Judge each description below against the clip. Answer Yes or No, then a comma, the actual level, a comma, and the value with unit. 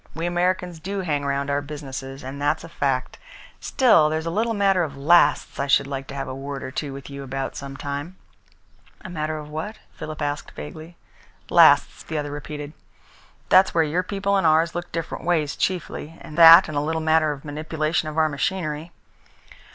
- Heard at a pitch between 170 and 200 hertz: No, medium, 155 Hz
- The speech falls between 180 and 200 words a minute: Yes, average, 195 wpm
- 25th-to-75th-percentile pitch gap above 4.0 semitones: No, average, 3.0 semitones